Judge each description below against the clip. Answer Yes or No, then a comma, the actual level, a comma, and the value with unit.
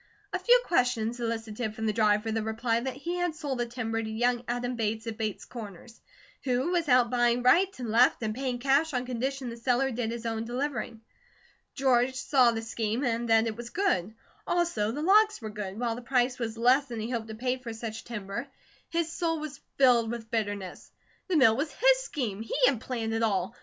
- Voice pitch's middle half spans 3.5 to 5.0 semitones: No, average, 2.9 semitones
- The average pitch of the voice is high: Yes, high, 240 Hz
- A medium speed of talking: No, fast, 210 wpm